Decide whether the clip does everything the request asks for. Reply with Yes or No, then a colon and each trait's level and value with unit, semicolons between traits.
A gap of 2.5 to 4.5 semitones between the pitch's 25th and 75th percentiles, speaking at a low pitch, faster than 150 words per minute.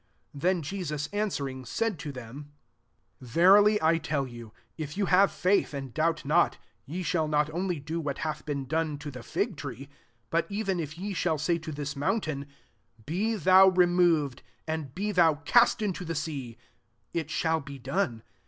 No: average, 4.2 semitones; medium, 160 Hz; average, 190 wpm